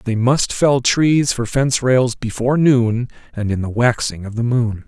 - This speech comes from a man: Yes, male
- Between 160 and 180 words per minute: No, average, 195 wpm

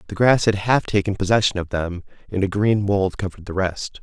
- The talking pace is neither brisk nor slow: No, fast, 225 wpm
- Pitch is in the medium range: No, low, 100 Hz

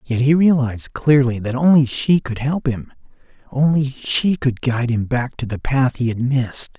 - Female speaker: No, male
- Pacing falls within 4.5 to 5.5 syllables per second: Yes, 4.8 syllables/s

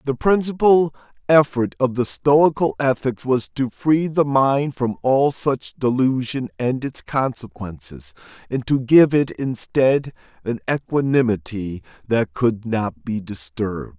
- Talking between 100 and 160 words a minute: Yes, slow, 135 wpm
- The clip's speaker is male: Yes, male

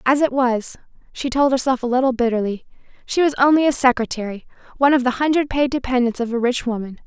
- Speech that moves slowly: No, fast, 205 wpm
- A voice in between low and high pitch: No, very high, 255 Hz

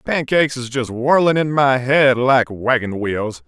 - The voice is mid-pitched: No, low, 130 Hz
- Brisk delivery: No, average, 175 wpm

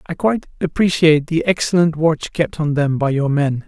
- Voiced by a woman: No, male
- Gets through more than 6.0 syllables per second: No, 5.3 syllables/s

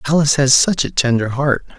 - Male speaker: Yes, male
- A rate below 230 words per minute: Yes, average, 200 wpm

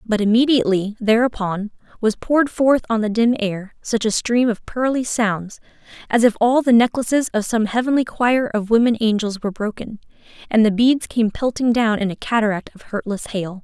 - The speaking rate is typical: Yes, average, 185 wpm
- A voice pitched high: Yes, high, 225 Hz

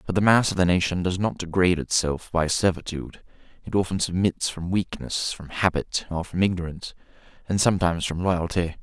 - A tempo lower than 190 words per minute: Yes, average, 175 wpm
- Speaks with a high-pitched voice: No, very low, 90 Hz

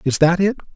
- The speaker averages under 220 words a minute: No, fast, 240 wpm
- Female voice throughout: No, male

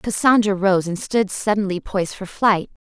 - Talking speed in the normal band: Yes, average, 165 wpm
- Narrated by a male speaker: No, female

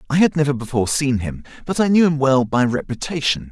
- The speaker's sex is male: Yes, male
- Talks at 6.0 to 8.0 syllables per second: Yes, 6.1 syllables/s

